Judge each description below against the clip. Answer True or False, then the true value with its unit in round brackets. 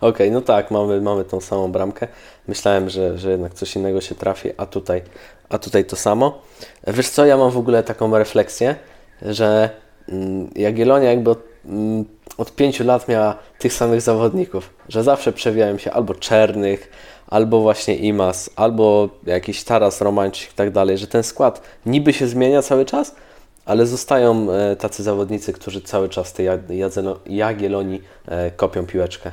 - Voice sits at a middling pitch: False (105 Hz)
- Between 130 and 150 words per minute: False (160 wpm)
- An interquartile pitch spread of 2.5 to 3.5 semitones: True (3.2 semitones)